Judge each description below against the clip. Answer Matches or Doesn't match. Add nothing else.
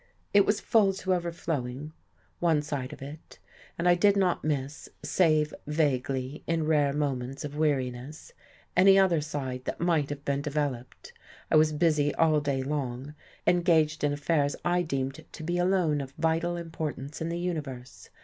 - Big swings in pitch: Doesn't match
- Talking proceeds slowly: Doesn't match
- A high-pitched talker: Doesn't match